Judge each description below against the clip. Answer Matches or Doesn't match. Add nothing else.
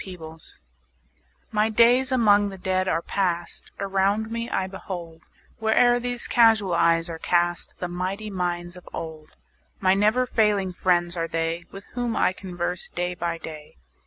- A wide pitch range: Doesn't match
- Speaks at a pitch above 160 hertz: Matches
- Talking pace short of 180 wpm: Matches